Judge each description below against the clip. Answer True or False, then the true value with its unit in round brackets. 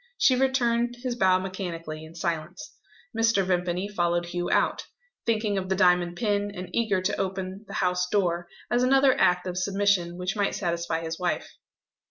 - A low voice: False (185 Hz)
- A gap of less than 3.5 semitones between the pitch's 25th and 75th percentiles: True (2.9 semitones)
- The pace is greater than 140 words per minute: True (170 wpm)